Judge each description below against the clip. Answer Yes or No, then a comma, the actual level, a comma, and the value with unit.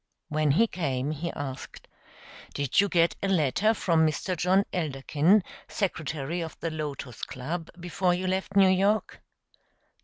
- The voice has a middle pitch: Yes, medium, 170 Hz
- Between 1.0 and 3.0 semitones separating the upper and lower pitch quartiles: No, average, 4.1 semitones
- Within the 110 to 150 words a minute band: Yes, average, 145 wpm